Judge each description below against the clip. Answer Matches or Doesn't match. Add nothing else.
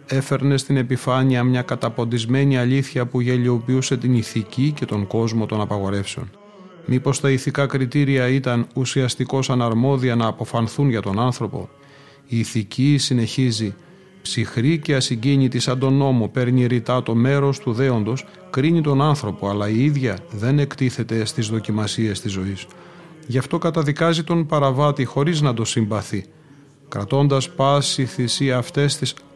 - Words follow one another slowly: Doesn't match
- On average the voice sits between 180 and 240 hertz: Doesn't match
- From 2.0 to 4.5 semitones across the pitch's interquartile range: Matches